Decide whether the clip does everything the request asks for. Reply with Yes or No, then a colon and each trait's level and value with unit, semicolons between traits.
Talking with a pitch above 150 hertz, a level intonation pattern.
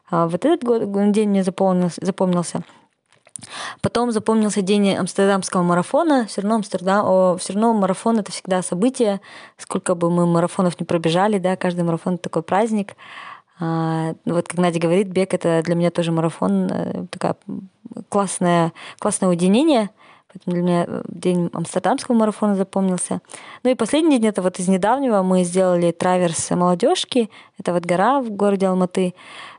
No: high, 190 Hz; average, 3.4 semitones